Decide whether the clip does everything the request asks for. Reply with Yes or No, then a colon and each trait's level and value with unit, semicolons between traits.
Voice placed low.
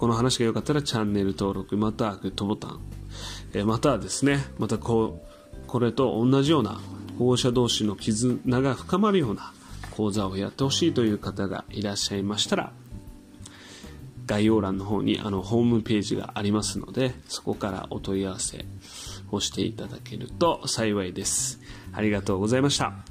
Yes: low, 105 Hz